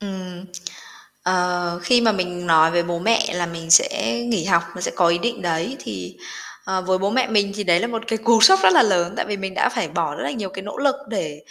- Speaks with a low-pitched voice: No, medium, 185 Hz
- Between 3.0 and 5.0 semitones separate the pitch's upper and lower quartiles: Yes, average, 4.3 semitones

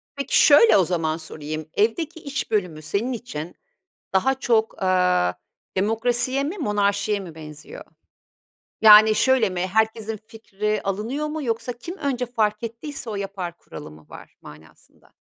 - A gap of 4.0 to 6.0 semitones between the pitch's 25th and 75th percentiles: Yes, average, 5.2 semitones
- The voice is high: Yes, high, 215 Hz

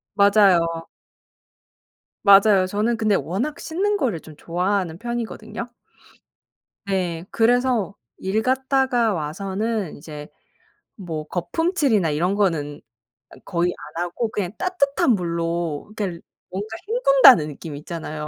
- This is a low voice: No, high, 195 Hz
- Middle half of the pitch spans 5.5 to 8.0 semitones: Yes, wide, 5.8 semitones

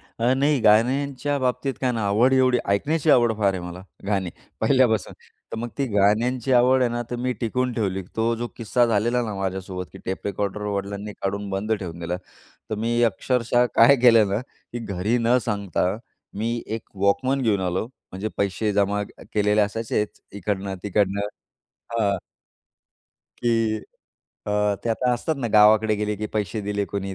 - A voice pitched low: Yes, low, 110 Hz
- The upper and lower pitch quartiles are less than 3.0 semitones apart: No, average, 3.3 semitones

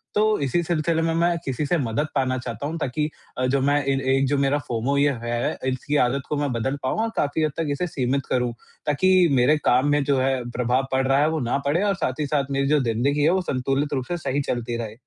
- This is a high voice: No, medium, 140 Hz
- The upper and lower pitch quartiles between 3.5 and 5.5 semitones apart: No, average, 2.9 semitones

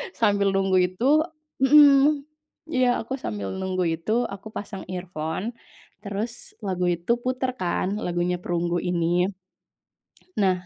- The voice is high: Yes, high, 195 Hz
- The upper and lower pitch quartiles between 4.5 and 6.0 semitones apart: Yes, average, 5.2 semitones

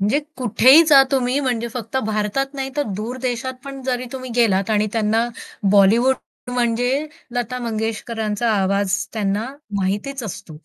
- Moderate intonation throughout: Yes, average, 3.5 semitones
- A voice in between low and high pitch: No, high, 235 Hz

